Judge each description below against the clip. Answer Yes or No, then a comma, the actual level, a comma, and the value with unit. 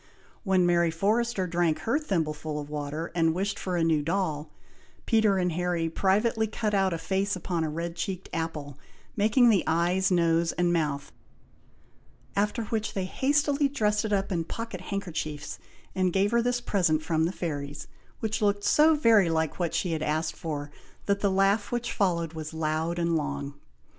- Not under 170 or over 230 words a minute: Yes, average, 175 wpm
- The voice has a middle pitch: Yes, medium, 180 Hz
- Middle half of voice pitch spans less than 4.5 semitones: Yes, average, 4.1 semitones